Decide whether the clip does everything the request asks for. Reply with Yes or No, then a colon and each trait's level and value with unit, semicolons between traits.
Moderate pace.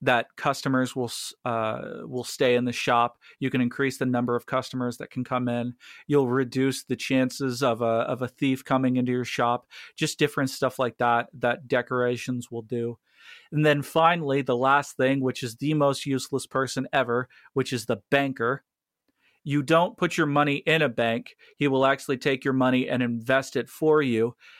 Yes: average, 190 wpm